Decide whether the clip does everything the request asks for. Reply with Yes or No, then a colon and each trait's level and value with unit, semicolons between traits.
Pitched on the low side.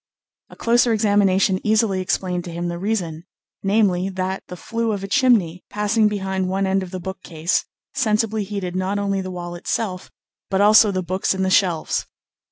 No: high, 190 Hz